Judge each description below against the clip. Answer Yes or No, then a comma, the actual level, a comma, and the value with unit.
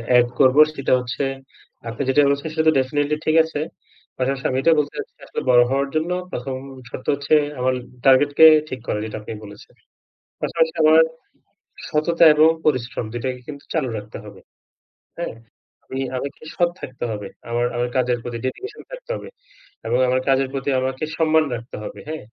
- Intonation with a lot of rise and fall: No, average, 3.8 semitones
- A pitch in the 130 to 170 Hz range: Yes, low, 135 Hz